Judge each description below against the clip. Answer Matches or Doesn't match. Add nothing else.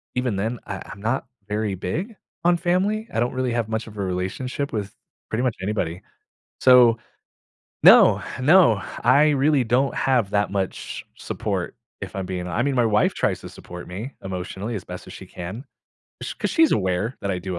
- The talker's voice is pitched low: Matches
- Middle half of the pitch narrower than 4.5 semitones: Doesn't match